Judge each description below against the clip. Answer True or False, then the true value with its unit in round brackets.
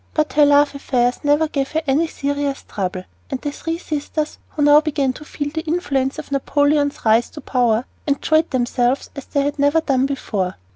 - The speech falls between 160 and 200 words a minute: True (190 wpm)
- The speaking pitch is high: True (285 Hz)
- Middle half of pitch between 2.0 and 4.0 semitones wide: True (2.4 semitones)